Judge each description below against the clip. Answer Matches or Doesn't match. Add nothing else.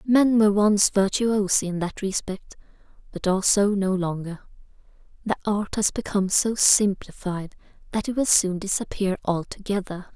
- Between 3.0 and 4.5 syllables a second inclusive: Doesn't match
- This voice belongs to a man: Doesn't match